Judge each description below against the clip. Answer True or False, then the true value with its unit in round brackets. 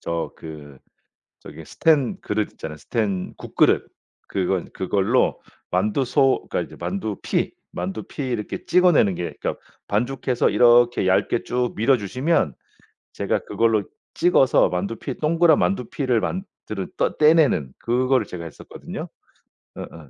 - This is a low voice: True (115 Hz)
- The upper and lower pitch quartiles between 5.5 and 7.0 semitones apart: True (6.0 semitones)